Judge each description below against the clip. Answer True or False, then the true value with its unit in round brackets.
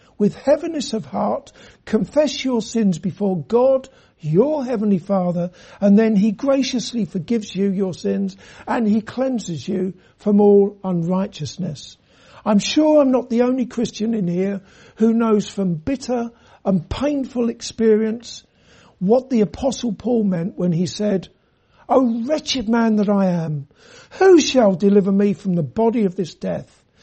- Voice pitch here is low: False (210 Hz)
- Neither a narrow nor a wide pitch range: True (4.2 semitones)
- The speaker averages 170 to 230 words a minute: False (150 wpm)